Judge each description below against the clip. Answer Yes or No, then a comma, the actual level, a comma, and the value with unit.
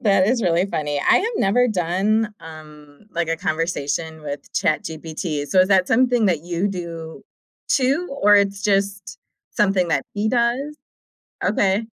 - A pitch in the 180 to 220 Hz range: Yes, high, 190 Hz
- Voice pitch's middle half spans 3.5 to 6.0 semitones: Yes, average, 4.6 semitones